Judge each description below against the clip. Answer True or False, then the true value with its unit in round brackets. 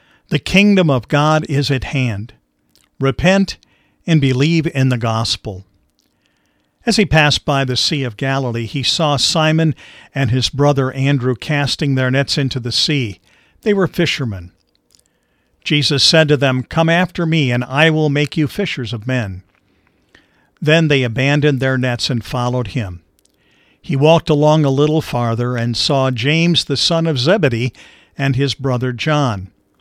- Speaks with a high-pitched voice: False (135 Hz)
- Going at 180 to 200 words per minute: False (155 wpm)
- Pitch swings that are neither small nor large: True (3.9 semitones)